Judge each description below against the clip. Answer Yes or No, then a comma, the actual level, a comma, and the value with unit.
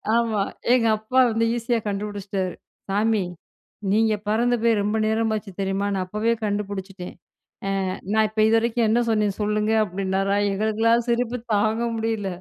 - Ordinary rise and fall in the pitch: No, narrow, 2.1 semitones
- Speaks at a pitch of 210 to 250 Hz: Yes, high, 215 Hz